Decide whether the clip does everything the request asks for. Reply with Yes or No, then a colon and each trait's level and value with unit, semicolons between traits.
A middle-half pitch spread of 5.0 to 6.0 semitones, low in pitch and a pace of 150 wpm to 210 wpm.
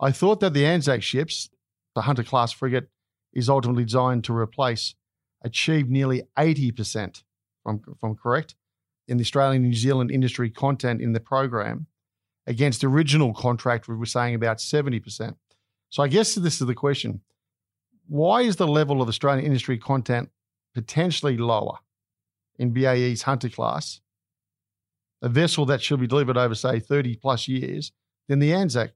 No: average, 3.7 semitones; low, 125 Hz; average, 160 wpm